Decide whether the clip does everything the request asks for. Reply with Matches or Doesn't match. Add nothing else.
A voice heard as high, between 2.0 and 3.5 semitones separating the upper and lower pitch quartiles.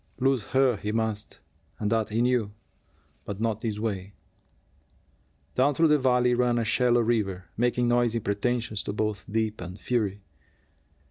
Doesn't match